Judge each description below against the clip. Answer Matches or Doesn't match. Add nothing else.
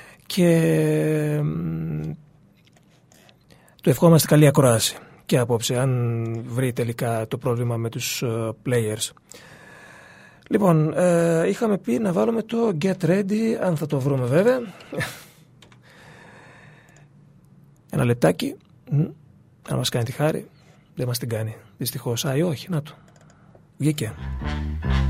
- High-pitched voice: Doesn't match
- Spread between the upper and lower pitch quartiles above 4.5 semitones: Matches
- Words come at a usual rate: Doesn't match